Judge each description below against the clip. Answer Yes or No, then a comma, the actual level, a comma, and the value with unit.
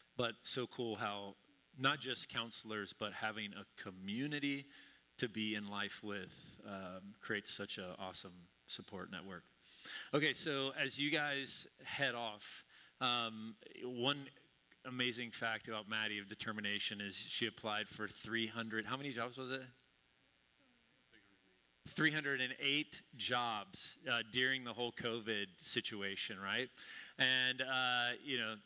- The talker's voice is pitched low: Yes, low, 115 Hz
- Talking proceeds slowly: Yes, slow, 130 wpm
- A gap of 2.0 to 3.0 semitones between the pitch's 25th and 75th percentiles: No, average, 3.9 semitones